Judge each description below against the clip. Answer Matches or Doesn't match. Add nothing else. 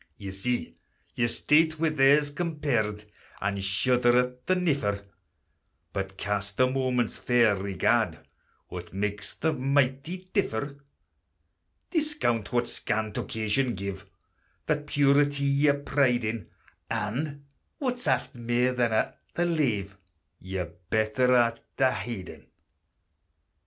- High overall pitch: Doesn't match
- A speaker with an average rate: Doesn't match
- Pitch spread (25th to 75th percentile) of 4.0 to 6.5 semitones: Matches